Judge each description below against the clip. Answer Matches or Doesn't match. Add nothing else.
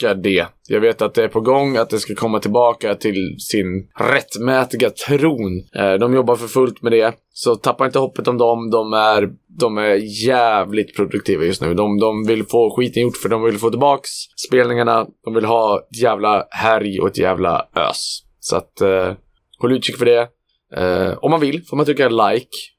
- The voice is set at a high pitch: Doesn't match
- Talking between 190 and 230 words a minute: Matches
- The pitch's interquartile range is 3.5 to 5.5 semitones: Doesn't match